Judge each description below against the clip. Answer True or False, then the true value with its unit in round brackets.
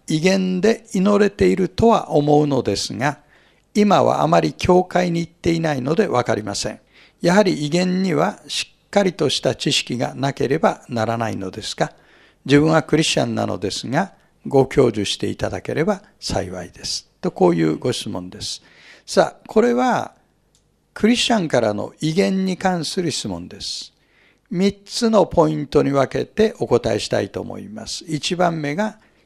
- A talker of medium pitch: True (160 Hz)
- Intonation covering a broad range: True (7.5 semitones)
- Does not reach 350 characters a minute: True (320 characters per minute)